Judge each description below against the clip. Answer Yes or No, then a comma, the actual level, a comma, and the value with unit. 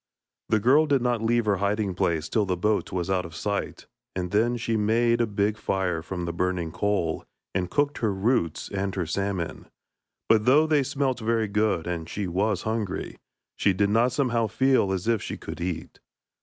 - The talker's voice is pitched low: Yes, low, 105 Hz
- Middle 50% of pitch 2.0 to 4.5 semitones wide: Yes, average, 4.2 semitones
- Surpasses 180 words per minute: Yes, average, 195 wpm